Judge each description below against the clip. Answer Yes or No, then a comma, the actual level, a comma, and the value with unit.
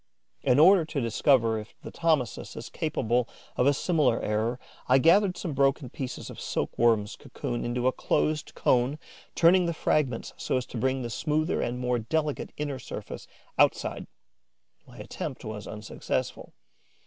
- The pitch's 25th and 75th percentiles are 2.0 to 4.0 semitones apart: No, average, 4.5 semitones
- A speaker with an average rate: Yes, average, 160 wpm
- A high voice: No, low, 130 Hz